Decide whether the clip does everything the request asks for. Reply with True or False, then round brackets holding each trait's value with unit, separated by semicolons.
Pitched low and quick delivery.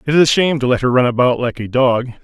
True (130 Hz; 320 wpm)